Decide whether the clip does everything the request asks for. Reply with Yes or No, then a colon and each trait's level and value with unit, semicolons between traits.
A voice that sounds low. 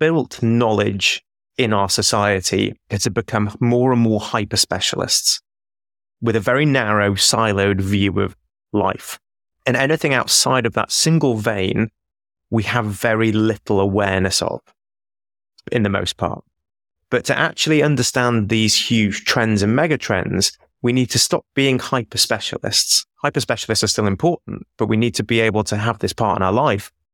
Yes: low, 110 Hz